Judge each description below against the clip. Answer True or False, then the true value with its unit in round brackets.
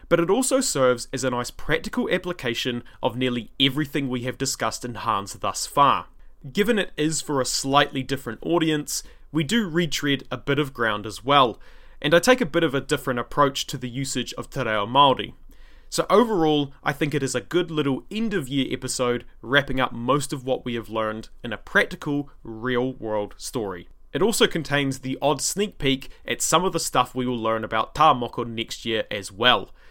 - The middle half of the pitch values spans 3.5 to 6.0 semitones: True (3.9 semitones)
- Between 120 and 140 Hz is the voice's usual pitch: True (135 Hz)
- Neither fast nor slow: True (195 wpm)